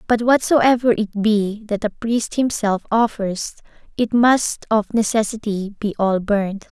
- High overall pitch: Yes, high, 215 Hz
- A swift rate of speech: No, average, 140 wpm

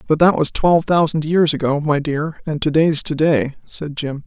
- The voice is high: No, medium, 155 Hz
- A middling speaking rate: No, fast, 225 wpm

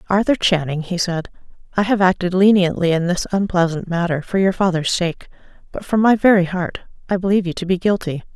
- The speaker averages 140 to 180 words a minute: No, average, 195 wpm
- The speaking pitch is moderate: Yes, medium, 180 Hz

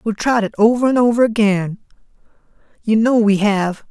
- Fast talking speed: No, average, 170 wpm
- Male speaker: Yes, male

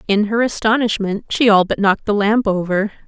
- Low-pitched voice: No, high, 210 Hz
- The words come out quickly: No, average, 195 wpm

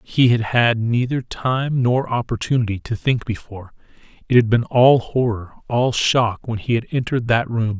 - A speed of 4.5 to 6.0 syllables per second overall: Yes, 4.7 syllables/s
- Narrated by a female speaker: No, male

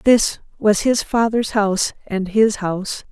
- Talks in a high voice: Yes, high, 210 Hz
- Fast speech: No, average, 155 wpm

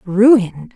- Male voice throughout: No, female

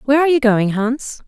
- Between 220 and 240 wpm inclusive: Yes, fast, 235 wpm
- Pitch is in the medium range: No, very high, 250 Hz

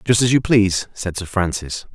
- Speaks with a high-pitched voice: No, low, 100 Hz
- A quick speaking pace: Yes, fast, 215 wpm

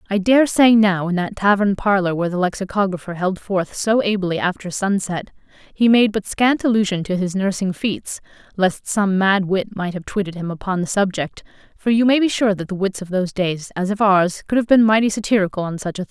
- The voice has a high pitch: Yes, high, 195 Hz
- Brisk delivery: Yes, fast, 225 wpm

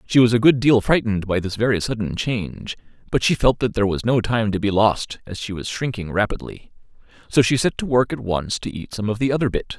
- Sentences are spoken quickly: Yes, fast, 250 wpm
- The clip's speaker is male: Yes, male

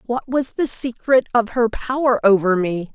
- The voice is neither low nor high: No, high, 235 Hz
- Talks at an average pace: Yes, average, 185 wpm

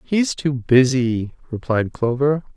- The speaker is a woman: No, male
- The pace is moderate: No, slow, 115 wpm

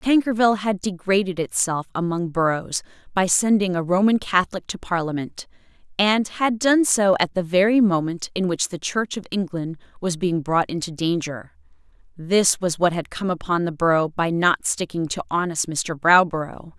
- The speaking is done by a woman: Yes, female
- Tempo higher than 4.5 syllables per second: Yes, 4.8 syllables/s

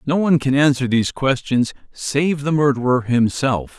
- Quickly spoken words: No, average, 160 wpm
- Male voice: Yes, male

